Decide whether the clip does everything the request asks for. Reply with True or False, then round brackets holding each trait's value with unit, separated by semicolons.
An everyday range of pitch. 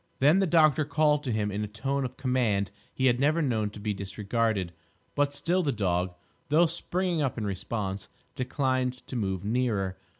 False (5.8 semitones)